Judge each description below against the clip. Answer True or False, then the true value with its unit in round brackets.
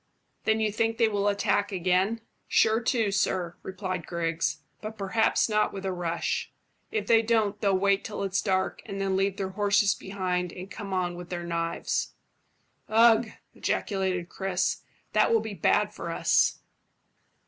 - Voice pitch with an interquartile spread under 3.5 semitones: True (2.8 semitones)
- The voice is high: True (195 Hz)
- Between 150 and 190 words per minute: True (160 wpm)